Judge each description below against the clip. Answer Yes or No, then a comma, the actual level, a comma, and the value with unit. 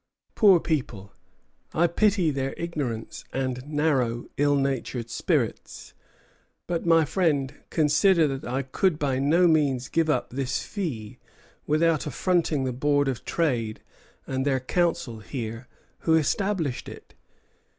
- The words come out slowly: Yes, slow, 130 wpm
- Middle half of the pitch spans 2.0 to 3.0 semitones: No, average, 4.2 semitones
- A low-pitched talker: No, medium, 145 Hz